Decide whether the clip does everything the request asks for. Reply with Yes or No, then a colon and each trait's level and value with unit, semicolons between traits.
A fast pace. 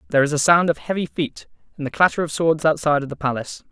Yes: fast, 260 wpm